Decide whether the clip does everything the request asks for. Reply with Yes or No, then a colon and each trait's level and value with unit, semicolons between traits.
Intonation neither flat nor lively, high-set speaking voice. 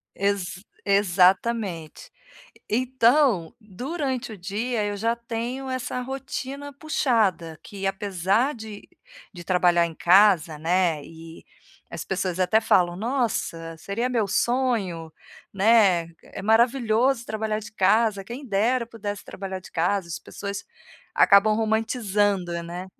Yes: average, 4.4 semitones; high, 205 Hz